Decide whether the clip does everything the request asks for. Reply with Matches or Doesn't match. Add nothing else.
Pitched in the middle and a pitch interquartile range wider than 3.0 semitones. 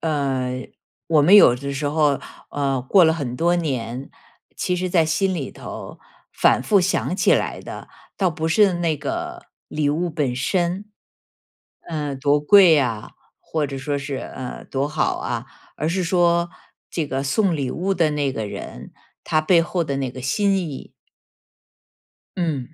Matches